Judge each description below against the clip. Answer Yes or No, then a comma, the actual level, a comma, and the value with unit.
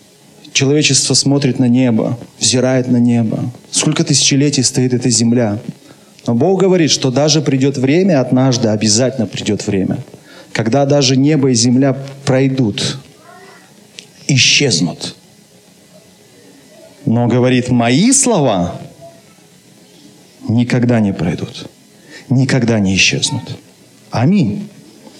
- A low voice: Yes, low, 130 Hz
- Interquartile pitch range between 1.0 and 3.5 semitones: Yes, average, 2.9 semitones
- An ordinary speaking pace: No, slow, 100 wpm